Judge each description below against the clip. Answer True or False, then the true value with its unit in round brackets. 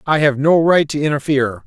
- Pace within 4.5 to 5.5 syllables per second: False (5.8 syllables/s)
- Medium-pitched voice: True (145 Hz)